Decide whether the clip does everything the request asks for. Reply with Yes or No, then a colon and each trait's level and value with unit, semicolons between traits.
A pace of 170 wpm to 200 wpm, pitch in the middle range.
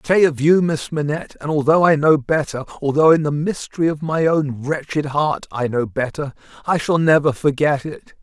Yes: average, 180 wpm; medium, 150 Hz